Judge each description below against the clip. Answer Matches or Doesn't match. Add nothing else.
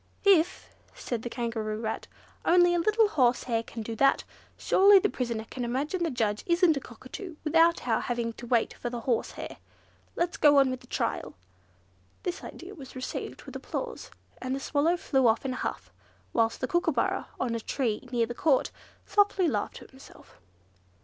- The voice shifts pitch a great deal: Matches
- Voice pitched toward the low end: Doesn't match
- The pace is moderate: Matches